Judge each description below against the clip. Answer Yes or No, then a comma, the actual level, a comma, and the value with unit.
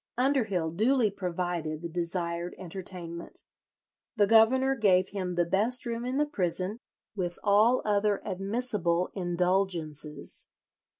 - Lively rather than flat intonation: No, average, 4.2 semitones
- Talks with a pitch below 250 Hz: Yes, high, 190 Hz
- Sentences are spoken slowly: Yes, slow, 115 wpm